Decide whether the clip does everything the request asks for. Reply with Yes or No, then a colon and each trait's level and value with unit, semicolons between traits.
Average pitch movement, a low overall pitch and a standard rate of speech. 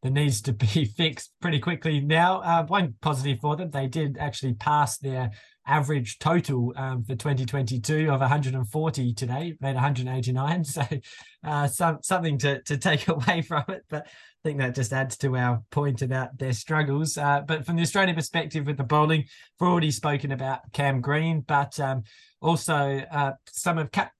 No: average, 3.0 semitones; medium, 145 Hz; average, 180 wpm